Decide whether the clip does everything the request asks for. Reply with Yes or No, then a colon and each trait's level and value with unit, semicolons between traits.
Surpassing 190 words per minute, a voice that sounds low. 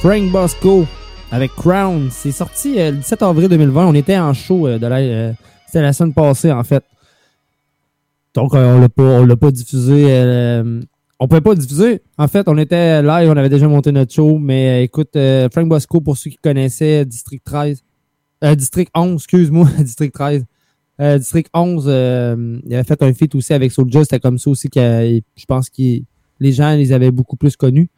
No: average, 205 wpm; medium, 145 Hz